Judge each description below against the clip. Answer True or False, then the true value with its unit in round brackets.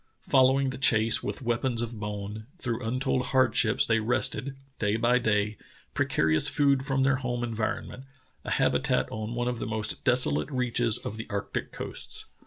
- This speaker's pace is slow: False (170 wpm)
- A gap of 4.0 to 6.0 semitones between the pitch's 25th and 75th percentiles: False (3.0 semitones)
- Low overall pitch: True (120 Hz)